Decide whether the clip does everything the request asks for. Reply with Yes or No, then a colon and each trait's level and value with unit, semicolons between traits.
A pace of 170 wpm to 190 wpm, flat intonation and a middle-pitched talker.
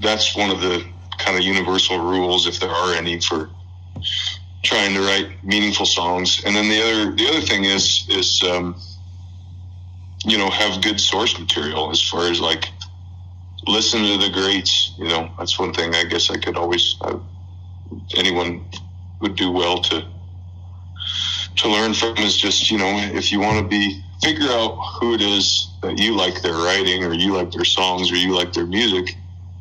No: average, 180 wpm; narrow, 1.5 semitones; very low, 90 Hz